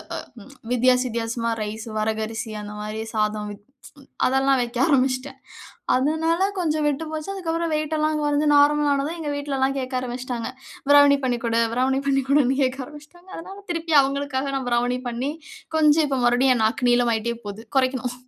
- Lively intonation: No, average, 3.6 semitones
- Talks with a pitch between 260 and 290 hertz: Yes, very high, 265 Hz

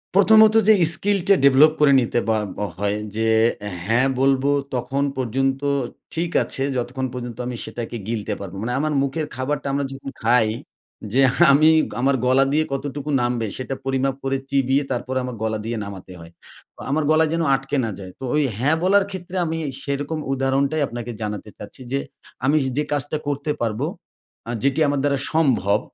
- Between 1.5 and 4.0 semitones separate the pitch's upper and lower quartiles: Yes, average, 3.3 semitones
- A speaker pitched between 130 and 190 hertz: Yes, low, 135 Hz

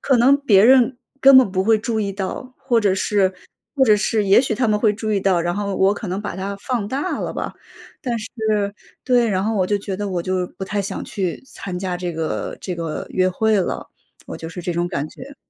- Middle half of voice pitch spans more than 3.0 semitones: Yes, average, 3.5 semitones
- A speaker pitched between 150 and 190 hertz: No, high, 200 Hz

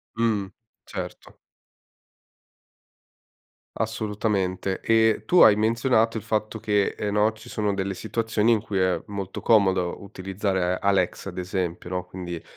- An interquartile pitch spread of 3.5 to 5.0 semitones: No, average, 2.7 semitones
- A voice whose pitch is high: No, low, 100 Hz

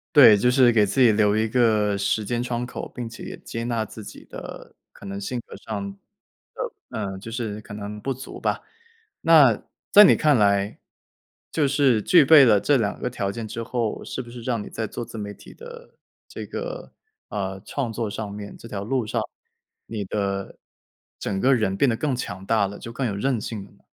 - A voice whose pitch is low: Yes, low, 115 Hz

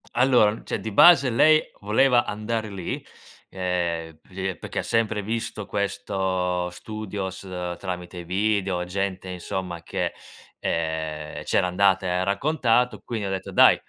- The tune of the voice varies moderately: Yes, average, 3.2 semitones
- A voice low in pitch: Yes, very low, 95 Hz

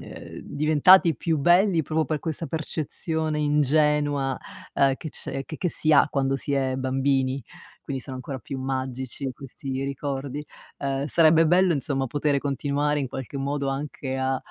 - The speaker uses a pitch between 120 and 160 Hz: Yes, medium, 140 Hz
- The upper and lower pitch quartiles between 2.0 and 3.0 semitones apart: Yes, narrow, 2.5 semitones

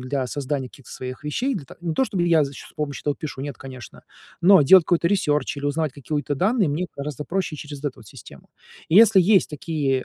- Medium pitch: Yes, medium, 150 Hz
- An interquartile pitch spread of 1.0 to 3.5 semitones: No, average, 4.1 semitones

